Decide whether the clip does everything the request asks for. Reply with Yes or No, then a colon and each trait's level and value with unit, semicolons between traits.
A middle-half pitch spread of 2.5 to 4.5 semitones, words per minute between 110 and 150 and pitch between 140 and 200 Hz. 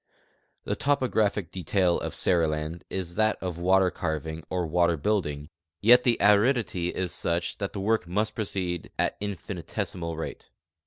No: average, 3.5 semitones; average, 145 wpm; very low, 90 Hz